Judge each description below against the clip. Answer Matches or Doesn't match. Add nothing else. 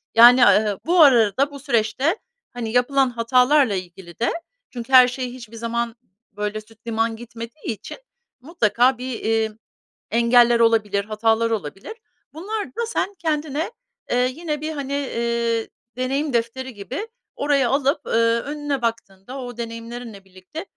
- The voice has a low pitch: Doesn't match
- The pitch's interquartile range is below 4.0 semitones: Matches